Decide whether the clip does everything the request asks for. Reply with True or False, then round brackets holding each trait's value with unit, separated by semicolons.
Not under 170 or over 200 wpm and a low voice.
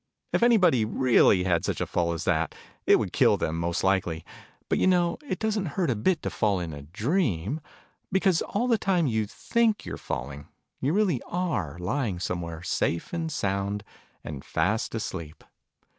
True (175 wpm; 110 Hz)